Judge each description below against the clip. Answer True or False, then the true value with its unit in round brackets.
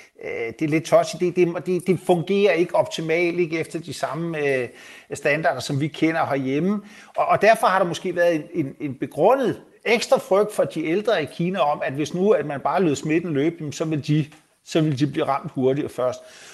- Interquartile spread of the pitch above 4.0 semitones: False (3.3 semitones)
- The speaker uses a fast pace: False (215 wpm)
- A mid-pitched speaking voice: True (165 Hz)